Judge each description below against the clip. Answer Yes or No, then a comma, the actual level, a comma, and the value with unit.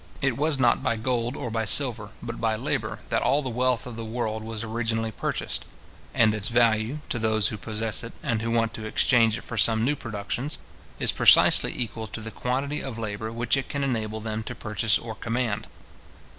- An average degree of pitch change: No, narrow, 2.0 semitones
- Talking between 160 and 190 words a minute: No, fast, 205 wpm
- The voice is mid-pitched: No, low, 115 Hz